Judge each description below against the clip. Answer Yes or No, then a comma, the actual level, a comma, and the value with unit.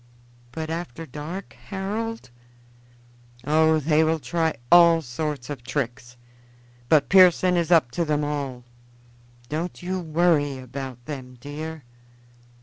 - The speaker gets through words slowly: Yes, slow, 120 wpm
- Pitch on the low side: No, medium, 155 Hz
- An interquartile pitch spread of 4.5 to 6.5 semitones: No, average, 3.7 semitones